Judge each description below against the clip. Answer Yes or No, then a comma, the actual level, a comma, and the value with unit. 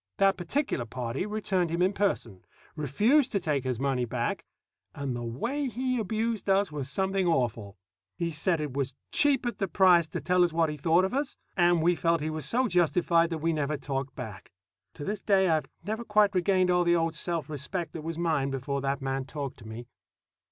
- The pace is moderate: No, fast, 210 wpm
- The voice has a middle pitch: Yes, medium, 165 Hz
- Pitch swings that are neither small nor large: No, wide, 5.7 semitones